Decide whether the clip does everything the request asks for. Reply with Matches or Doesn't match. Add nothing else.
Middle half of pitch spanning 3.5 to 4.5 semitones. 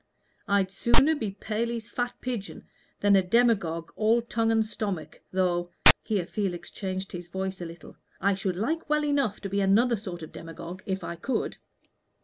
Matches